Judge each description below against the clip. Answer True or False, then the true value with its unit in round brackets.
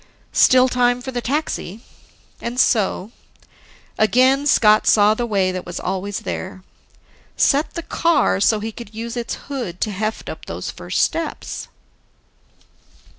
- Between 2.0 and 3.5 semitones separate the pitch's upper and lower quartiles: False (3.9 semitones)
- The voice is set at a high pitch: True (230 Hz)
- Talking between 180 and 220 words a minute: False (140 wpm)